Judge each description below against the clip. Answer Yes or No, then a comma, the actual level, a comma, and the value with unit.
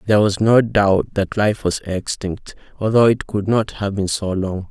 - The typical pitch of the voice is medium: No, low, 100 Hz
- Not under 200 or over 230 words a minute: Yes, fast, 205 wpm